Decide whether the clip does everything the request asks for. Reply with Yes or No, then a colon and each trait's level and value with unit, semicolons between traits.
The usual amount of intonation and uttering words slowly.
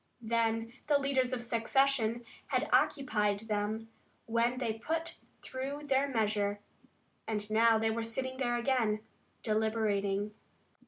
Yes: average, 3.1 semitones; slow, 120 wpm